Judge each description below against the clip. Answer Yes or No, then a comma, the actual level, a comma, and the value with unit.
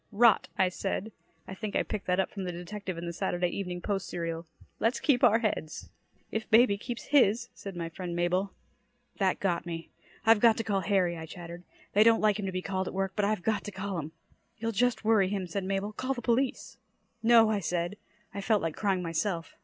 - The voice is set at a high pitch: Yes, high, 195 Hz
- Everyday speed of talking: No, fast, 220 wpm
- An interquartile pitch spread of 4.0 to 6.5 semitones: No, average, 3.5 semitones